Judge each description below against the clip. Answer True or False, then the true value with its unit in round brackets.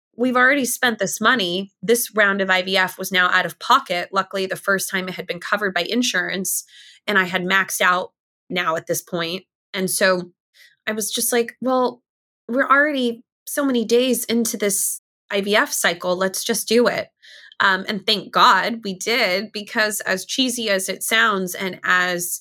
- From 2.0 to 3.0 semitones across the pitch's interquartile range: False (4.0 semitones)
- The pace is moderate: True (180 wpm)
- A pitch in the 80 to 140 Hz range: False (195 Hz)